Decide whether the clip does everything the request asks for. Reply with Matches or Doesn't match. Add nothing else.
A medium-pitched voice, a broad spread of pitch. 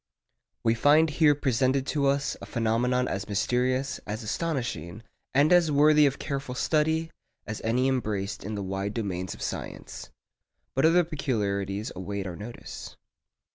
Doesn't match